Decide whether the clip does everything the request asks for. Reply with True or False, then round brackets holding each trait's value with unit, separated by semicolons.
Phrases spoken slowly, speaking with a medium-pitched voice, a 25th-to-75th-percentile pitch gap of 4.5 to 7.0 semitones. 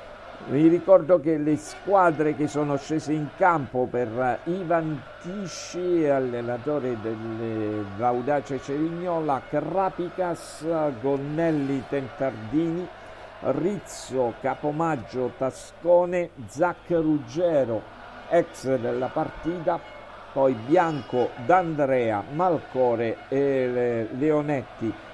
True (80 wpm; 150 Hz; 4.9 semitones)